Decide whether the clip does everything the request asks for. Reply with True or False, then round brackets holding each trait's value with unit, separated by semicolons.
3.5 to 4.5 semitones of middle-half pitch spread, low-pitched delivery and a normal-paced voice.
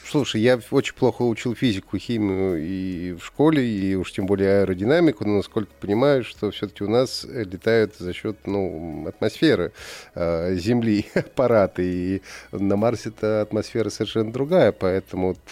True (3.8 semitones; 105 Hz; 145 wpm)